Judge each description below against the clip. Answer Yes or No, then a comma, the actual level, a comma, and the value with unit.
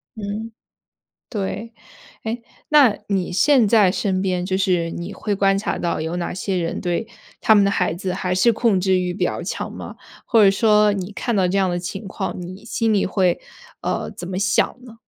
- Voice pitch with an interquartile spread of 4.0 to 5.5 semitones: No, average, 2.8 semitones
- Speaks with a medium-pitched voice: No, high, 195 Hz